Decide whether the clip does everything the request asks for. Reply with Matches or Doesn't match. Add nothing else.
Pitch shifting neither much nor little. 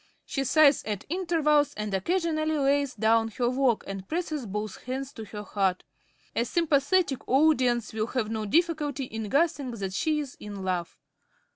Doesn't match